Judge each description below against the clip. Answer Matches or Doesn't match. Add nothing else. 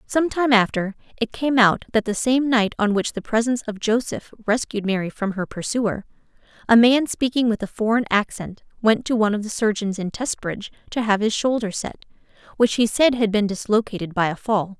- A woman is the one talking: Matches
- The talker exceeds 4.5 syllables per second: Matches